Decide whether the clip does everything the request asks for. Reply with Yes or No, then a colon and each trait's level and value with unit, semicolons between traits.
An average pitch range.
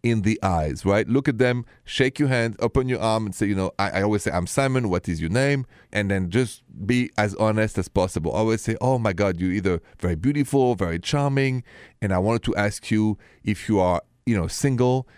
Yes: average, 4.3 semitones